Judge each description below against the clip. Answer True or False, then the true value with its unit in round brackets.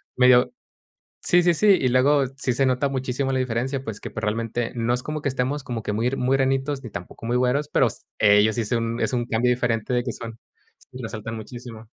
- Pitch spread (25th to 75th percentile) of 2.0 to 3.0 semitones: True (2.7 semitones)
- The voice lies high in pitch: False (125 Hz)